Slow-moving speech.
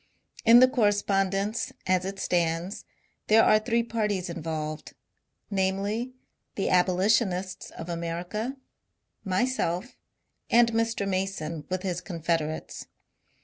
Yes: slow, 105 wpm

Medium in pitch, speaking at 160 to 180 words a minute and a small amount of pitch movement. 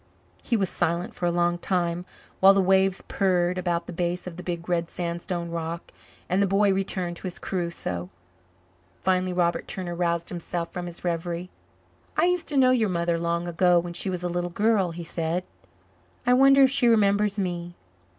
No: medium, 175 Hz; average, 190 wpm; narrow, 2.1 semitones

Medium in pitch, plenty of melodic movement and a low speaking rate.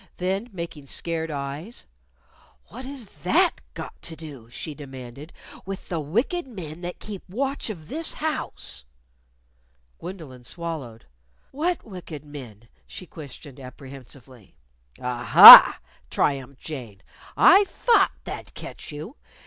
Yes: medium, 155 Hz; wide, 6.4 semitones; slow, 120 wpm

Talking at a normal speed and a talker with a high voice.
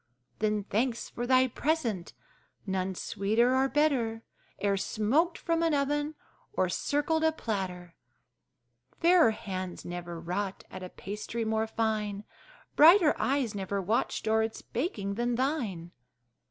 No: slow, 130 wpm; high, 220 Hz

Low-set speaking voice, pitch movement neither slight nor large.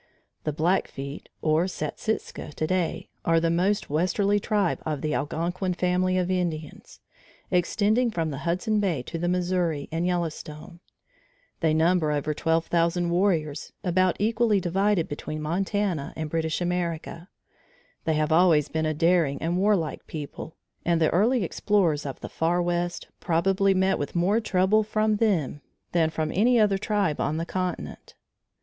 No: medium, 175 Hz; average, 3.2 semitones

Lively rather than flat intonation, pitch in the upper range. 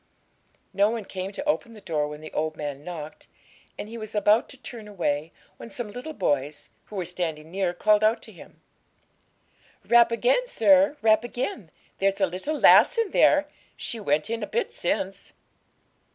Yes: wide, 5.7 semitones; high, 205 Hz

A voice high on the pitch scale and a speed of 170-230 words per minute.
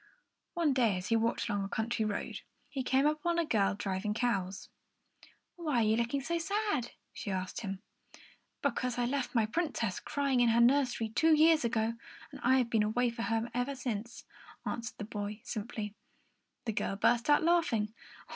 Yes: high, 235 Hz; average, 180 wpm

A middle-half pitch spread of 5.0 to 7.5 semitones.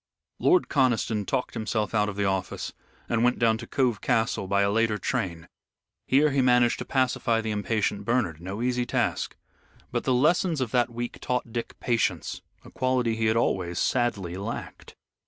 No: average, 3.5 semitones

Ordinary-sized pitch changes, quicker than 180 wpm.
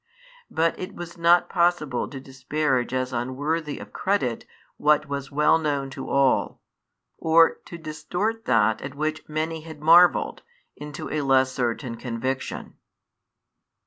No: average, 3.7 semitones; slow, 135 wpm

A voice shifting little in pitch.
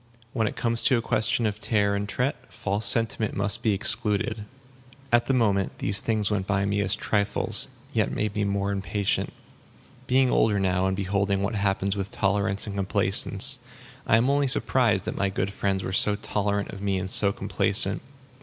Yes: narrow, 1.8 semitones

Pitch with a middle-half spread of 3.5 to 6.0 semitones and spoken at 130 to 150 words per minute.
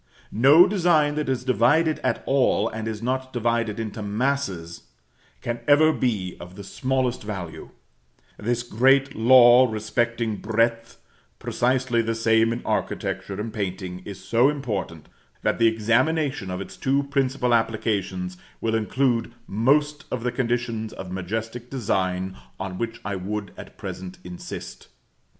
Yes: average, 4.0 semitones; average, 140 wpm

